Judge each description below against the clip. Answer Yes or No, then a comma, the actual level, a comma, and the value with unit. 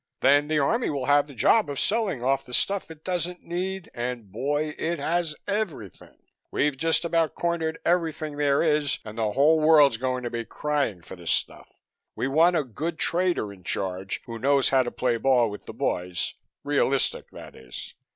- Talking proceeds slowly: No, average, 190 wpm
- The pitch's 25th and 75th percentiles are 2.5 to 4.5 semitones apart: No, average, 5.0 semitones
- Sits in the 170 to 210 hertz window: No, medium, 145 Hz